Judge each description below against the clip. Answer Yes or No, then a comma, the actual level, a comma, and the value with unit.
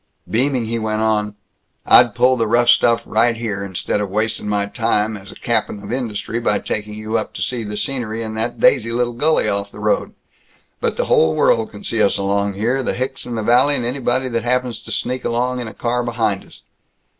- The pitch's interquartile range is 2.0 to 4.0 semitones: Yes, narrow, 2.6 semitones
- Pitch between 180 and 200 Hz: No, low, 115 Hz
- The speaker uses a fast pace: Yes, fast, 220 wpm